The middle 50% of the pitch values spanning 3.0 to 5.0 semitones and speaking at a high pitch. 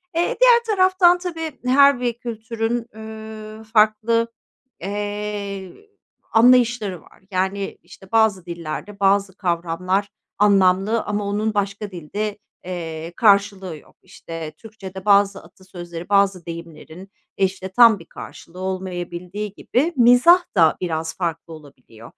Yes: average, 3.6 semitones; high, 200 Hz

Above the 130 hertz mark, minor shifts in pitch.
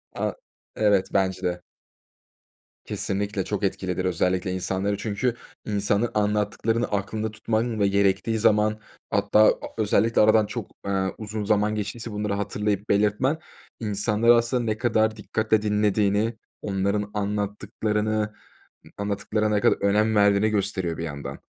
No: low, 105 Hz; narrow, 1.5 semitones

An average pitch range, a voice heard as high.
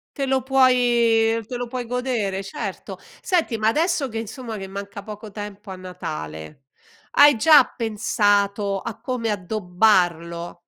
Yes: average, 4.0 semitones; high, 220 Hz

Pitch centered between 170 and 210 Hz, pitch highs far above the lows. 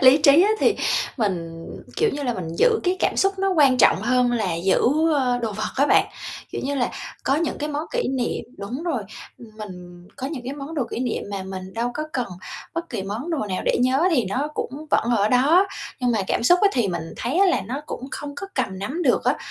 No: very high, 255 Hz; wide, 6.1 semitones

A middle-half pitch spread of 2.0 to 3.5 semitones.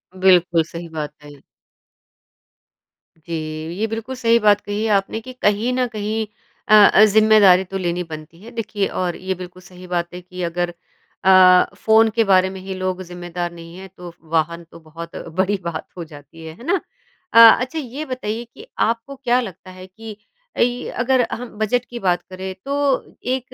No: average, 4.3 semitones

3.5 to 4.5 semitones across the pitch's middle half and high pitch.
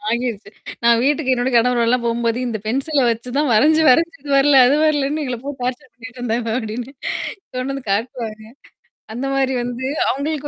No: average, 2.8 semitones; very high, 250 Hz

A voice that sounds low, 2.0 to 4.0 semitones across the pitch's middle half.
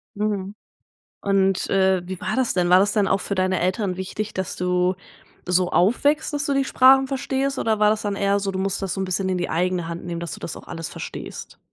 No: high, 195 Hz; average, 2.8 semitones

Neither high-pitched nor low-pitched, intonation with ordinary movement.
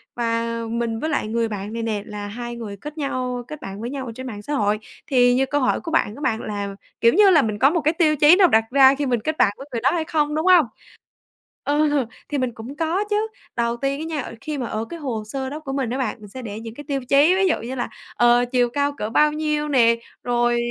No: very high, 255 Hz; average, 4.5 semitones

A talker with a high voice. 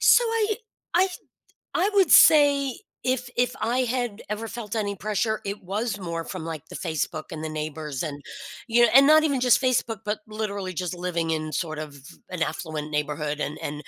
Yes: high, 205 Hz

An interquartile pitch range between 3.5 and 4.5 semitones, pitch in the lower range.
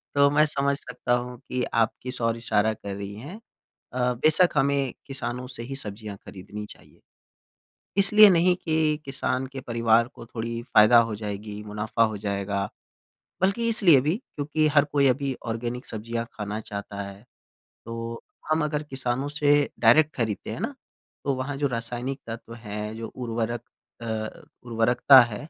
Yes: average, 4.2 semitones; low, 120 Hz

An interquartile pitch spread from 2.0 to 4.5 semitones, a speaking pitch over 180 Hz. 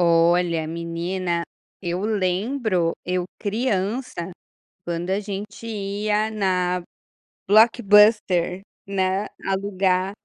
Yes: average, 2.8 semitones; high, 190 Hz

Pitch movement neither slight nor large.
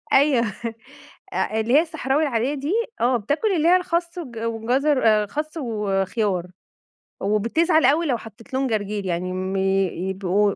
No: wide, 6.2 semitones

